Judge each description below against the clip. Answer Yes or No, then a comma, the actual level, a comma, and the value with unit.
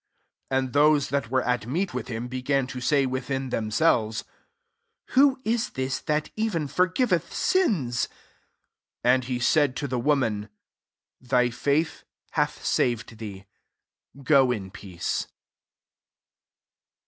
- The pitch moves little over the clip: No, average, 3.8 semitones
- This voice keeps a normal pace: No, slow, 130 wpm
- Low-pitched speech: Yes, low, 130 Hz